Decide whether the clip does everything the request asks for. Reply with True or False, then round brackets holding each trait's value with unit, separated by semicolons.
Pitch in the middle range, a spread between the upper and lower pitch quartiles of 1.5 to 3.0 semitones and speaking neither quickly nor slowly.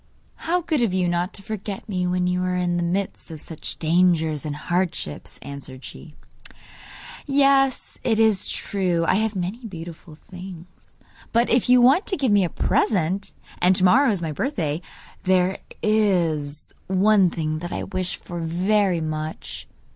False (180 Hz; 4.2 semitones; 165 wpm)